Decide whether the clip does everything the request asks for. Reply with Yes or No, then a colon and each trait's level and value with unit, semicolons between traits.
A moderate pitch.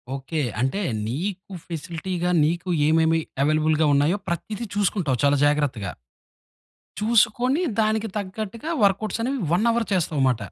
Yes: medium, 175 Hz